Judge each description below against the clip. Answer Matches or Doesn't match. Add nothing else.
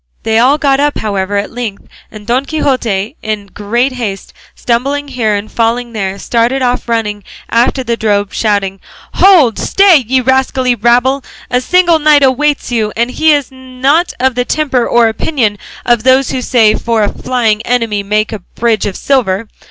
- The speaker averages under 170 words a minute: Doesn't match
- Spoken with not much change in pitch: Doesn't match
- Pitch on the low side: Doesn't match